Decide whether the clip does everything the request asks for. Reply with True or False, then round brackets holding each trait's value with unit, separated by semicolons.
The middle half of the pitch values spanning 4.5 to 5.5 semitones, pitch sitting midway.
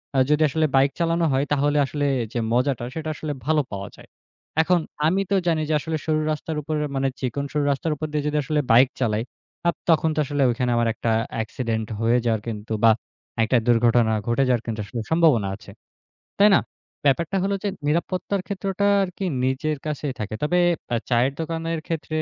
True (5.2 semitones; 145 Hz)